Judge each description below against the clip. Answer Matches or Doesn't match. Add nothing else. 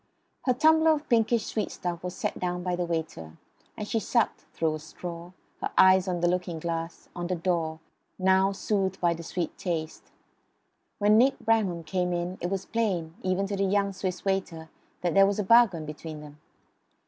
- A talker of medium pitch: Matches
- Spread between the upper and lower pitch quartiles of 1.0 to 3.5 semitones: Matches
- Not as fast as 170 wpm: Doesn't match